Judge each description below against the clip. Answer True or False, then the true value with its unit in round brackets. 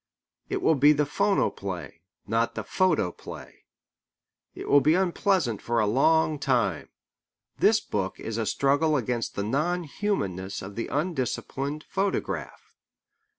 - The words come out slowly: True (130 wpm)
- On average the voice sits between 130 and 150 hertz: True (140 Hz)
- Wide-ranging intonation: True (6.7 semitones)